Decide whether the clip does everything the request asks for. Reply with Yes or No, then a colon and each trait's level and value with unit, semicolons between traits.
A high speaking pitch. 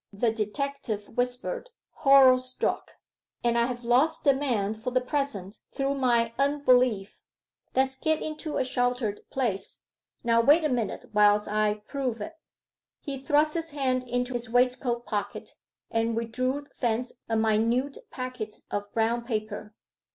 Yes: high, 245 Hz